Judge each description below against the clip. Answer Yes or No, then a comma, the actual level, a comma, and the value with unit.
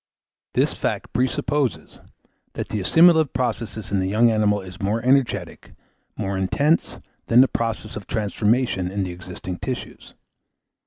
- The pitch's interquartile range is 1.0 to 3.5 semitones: No, average, 4.6 semitones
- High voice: No, low, 110 Hz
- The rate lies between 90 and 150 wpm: Yes, average, 140 wpm